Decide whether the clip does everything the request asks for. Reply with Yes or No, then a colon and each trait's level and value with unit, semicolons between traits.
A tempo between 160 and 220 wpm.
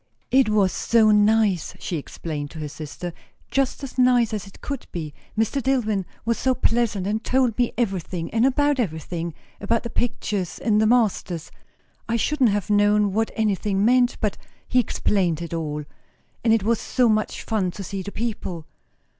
Yes: average, 170 wpm